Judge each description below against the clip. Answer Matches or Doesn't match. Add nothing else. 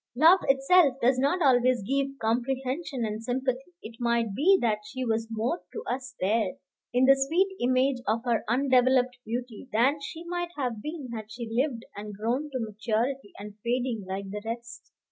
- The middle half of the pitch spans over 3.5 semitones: Doesn't match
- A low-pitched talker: Doesn't match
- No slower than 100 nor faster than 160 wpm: Doesn't match